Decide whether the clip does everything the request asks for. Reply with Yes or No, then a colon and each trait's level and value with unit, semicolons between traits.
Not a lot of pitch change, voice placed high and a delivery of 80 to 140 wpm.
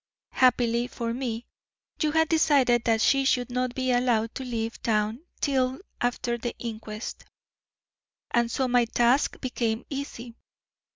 Yes: narrow, 2.0 semitones; high, 245 Hz; slow, 135 wpm